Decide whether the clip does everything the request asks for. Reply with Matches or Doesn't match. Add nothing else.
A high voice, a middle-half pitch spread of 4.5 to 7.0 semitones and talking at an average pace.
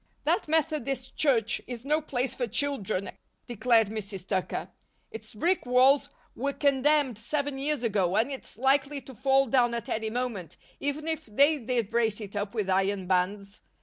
Matches